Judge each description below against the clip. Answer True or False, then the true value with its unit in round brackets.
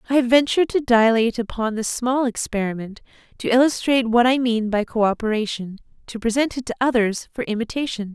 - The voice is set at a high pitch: True (235 Hz)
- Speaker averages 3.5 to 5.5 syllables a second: False (6.0 syllables/s)